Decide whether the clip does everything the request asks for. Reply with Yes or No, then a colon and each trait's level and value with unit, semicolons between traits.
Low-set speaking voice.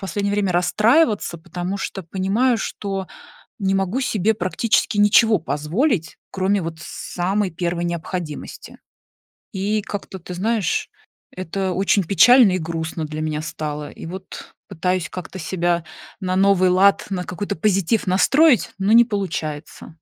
No: high, 190 Hz